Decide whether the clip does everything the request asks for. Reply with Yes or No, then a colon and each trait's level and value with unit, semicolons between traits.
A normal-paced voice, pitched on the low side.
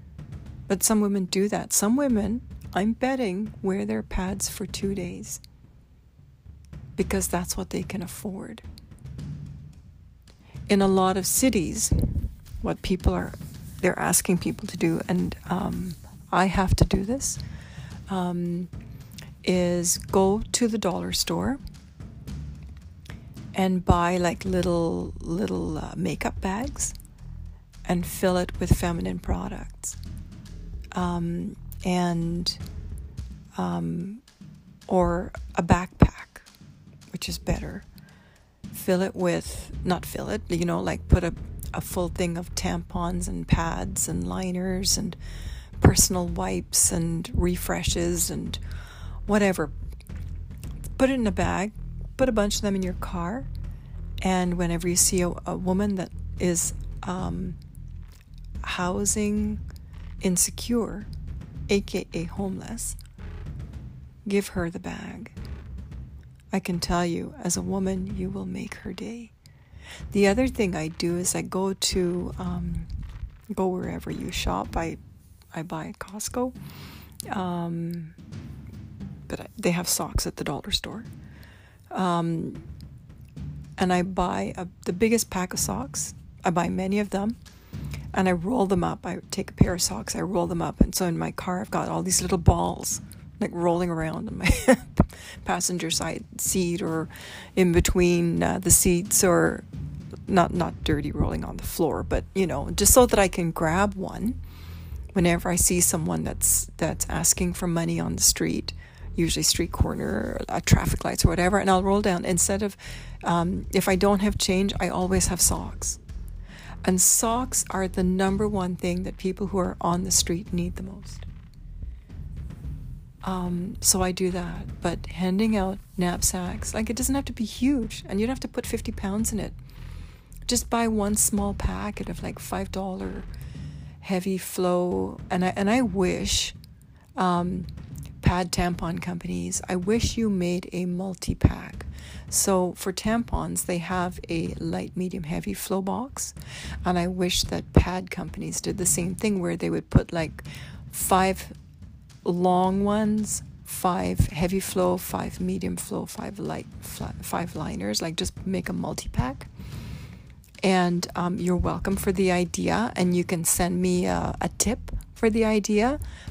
No: average, 150 wpm; medium, 180 Hz